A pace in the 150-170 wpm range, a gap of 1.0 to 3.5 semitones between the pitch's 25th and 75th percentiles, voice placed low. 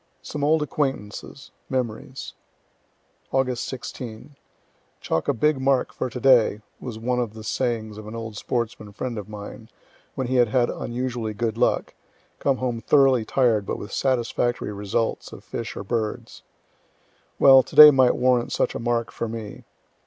Yes: average, 160 wpm; average, 3.0 semitones; low, 120 Hz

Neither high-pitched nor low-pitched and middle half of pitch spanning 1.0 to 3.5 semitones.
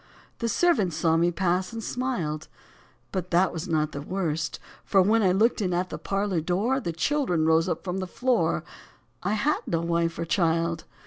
No: medium, 180 Hz; average, 3.9 semitones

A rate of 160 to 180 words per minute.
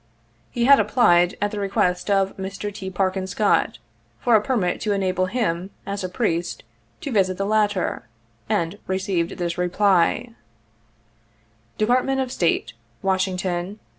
No: average, 145 wpm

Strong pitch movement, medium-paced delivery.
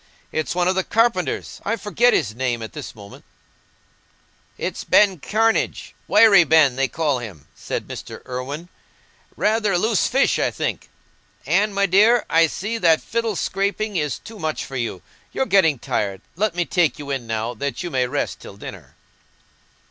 Yes: wide, 8.0 semitones; average, 165 wpm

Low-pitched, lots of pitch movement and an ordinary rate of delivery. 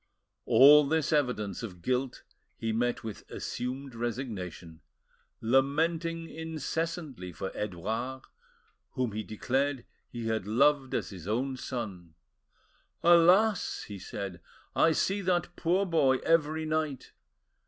No: low, 130 Hz; wide, 6.5 semitones; slow, 115 wpm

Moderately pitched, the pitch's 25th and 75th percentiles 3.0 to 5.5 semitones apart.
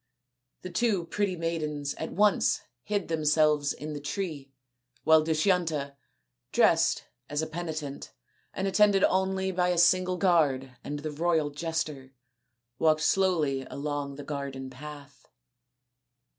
Yes: medium, 155 Hz; average, 3.8 semitones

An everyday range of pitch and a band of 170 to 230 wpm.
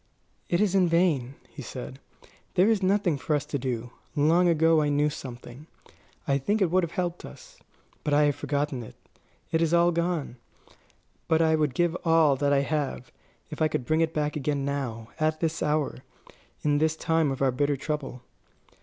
Yes: average, 3.0 semitones; average, 190 wpm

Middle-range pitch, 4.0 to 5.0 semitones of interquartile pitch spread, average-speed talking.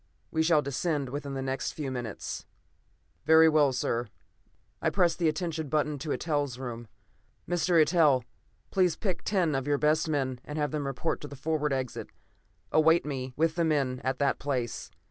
No: medium, 150 Hz; average, 3.2 semitones; average, 175 wpm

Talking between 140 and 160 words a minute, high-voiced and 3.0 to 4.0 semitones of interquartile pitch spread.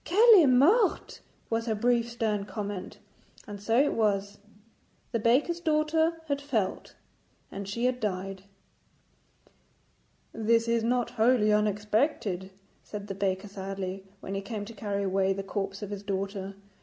Yes: average, 145 wpm; high, 210 Hz; average, 3.7 semitones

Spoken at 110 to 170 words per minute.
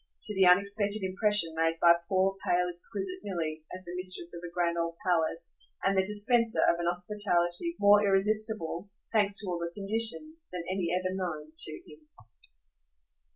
Yes: average, 165 wpm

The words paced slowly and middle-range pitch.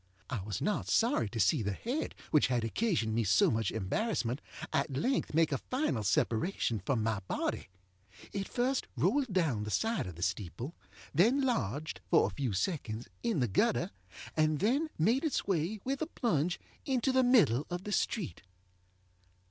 No: average, 170 wpm; medium, 155 Hz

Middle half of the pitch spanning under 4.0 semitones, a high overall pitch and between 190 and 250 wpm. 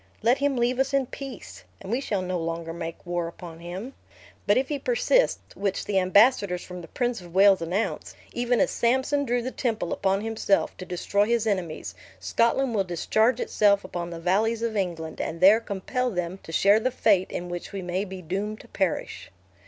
No: average, 5.0 semitones; high, 200 Hz; average, 200 wpm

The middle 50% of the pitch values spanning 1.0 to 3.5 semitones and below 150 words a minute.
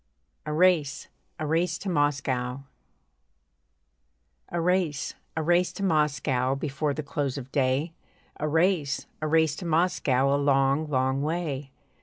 Yes: average, 3.1 semitones; slow, 135 wpm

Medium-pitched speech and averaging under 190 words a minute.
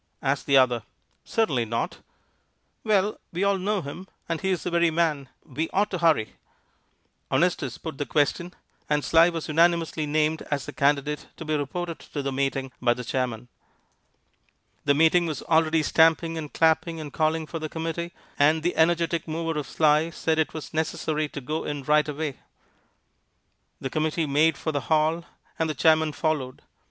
Yes: medium, 155 Hz; average, 175 wpm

